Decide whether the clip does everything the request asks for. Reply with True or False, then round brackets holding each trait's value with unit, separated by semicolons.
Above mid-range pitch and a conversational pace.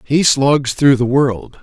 False (135 Hz; 185 wpm)